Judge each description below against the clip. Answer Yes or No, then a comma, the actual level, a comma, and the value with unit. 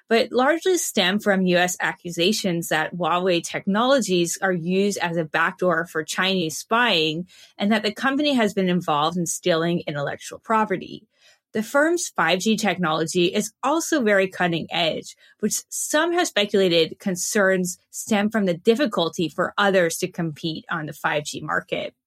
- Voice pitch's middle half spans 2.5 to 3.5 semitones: No, average, 4.2 semitones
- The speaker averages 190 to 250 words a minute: No, average, 145 wpm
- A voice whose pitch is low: No, medium, 185 Hz